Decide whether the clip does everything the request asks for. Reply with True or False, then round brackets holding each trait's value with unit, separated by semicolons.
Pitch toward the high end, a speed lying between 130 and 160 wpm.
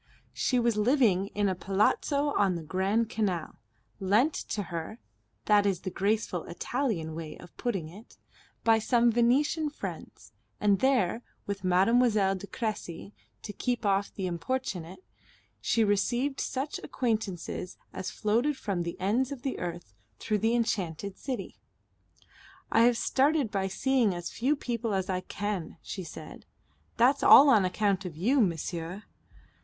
True (205 Hz; 150 wpm)